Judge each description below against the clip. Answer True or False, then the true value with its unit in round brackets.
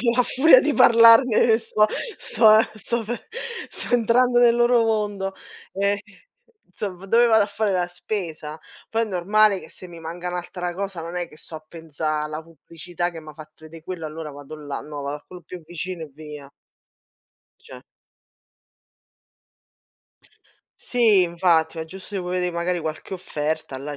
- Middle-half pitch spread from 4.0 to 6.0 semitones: True (5.1 semitones)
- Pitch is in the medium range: True (180 Hz)